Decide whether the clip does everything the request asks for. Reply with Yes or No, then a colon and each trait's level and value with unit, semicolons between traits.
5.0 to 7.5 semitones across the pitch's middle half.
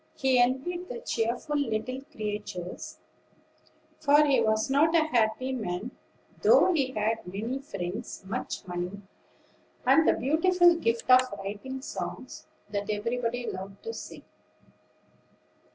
Yes: average, 5.3 semitones